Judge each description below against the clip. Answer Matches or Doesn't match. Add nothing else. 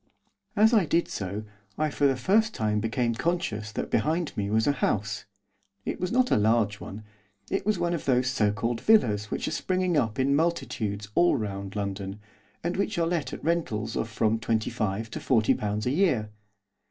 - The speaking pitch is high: Doesn't match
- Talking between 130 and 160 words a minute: Doesn't match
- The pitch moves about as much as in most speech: Doesn't match